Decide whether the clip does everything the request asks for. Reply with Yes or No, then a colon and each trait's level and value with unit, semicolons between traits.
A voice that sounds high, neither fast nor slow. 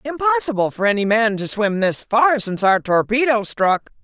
Yes: high, 220 Hz; average, 180 wpm